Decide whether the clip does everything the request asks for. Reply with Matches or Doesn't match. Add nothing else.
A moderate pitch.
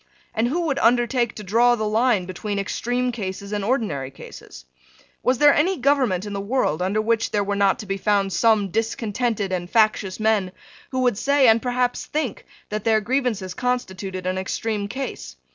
Doesn't match